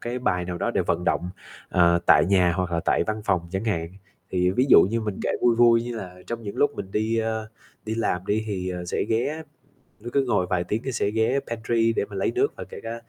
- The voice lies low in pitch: Yes, low, 110 Hz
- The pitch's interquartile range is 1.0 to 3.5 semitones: No, average, 4.1 semitones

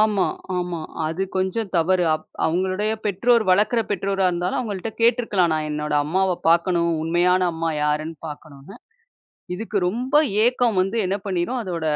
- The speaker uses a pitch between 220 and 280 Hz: No, medium, 185 Hz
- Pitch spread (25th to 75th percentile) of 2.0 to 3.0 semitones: No, average, 3.9 semitones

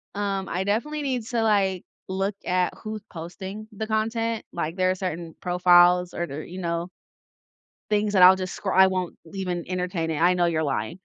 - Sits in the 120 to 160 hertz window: No, medium, 185 Hz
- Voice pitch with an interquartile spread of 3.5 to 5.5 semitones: No, average, 2.7 semitones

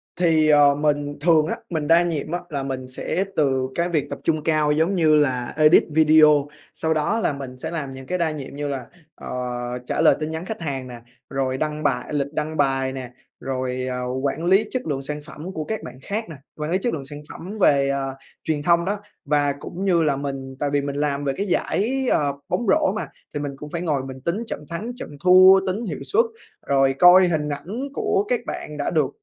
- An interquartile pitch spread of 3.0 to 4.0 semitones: Yes, average, 3.7 semitones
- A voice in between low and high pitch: Yes, medium, 150 Hz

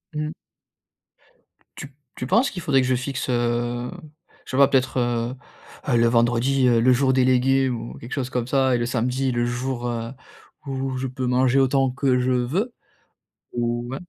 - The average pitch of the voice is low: Yes, low, 130 Hz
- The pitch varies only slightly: Yes, narrow, 1.8 semitones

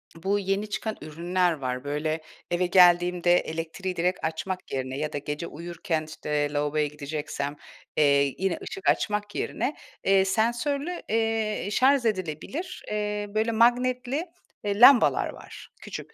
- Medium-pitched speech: Yes, medium, 180 Hz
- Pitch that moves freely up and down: Yes, wide, 5.7 semitones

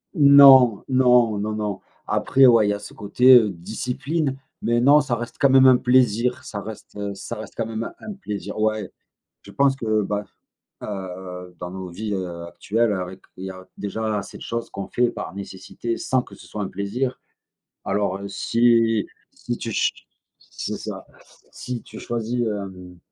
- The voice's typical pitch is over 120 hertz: No, low, 110 Hz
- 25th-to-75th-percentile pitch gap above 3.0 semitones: Yes, average, 3.7 semitones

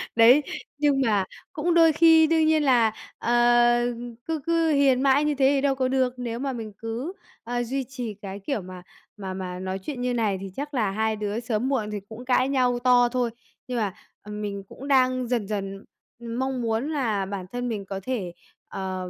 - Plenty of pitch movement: No, average, 4.3 semitones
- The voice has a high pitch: Yes, high, 245 Hz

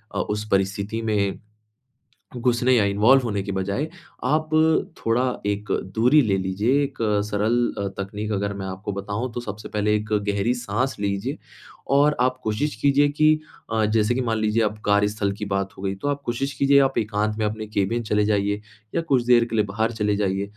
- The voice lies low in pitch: Yes, low, 105 Hz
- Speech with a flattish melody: No, average, 3.3 semitones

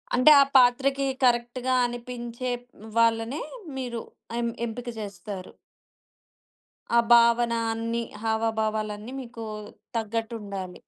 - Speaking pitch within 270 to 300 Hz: No, high, 235 Hz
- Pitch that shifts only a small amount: Yes, narrow, 1.7 semitones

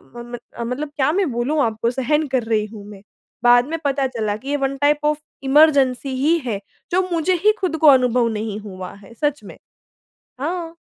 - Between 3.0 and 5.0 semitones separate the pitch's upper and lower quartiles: Yes, average, 4.4 semitones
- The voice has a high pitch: Yes, very high, 265 Hz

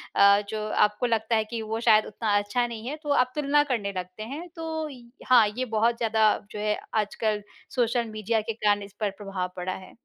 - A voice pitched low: No, high, 220 Hz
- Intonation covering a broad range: No, average, 2.8 semitones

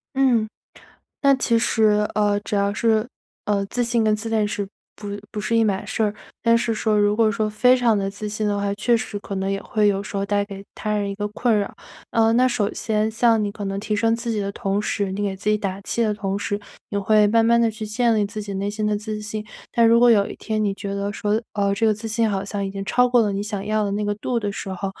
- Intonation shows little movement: Yes, narrow, 1.9 semitones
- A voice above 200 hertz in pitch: Yes, high, 210 Hz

